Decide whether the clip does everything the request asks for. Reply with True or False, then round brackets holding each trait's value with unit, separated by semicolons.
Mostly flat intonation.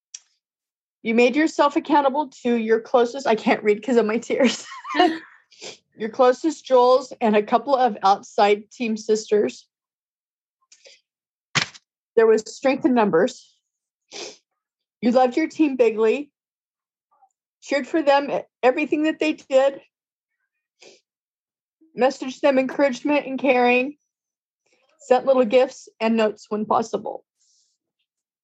False (4.4 semitones)